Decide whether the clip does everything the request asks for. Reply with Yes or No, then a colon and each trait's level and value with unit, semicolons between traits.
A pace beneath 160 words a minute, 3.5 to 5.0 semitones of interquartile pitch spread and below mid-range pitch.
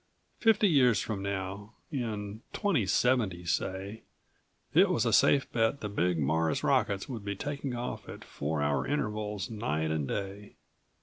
Yes: average, 145 wpm; average, 4.6 semitones; low, 105 Hz